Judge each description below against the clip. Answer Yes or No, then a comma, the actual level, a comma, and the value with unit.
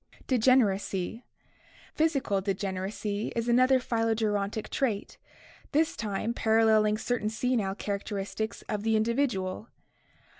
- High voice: Yes, high, 220 Hz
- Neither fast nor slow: No, slow, 105 wpm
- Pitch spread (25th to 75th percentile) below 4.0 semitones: Yes, average, 2.9 semitones